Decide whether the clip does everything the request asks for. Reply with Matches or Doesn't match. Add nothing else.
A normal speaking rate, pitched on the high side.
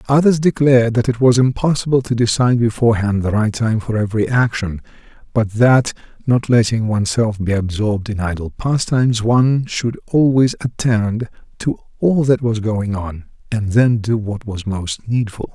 Doesn't match